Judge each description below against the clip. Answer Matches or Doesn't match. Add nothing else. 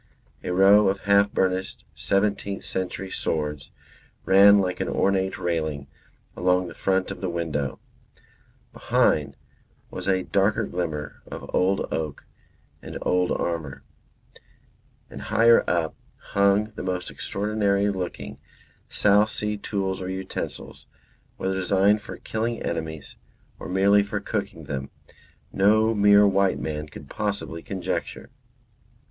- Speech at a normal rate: Doesn't match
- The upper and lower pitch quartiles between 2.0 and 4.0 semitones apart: Matches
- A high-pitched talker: Doesn't match